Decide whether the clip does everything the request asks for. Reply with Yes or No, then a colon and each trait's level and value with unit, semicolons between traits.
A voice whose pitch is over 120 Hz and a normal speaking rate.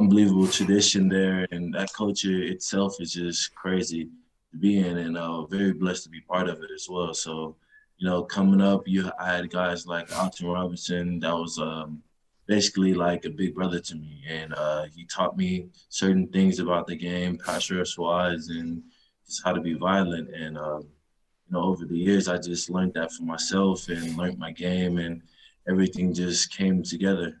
No: very low, 90 Hz; average, 190 wpm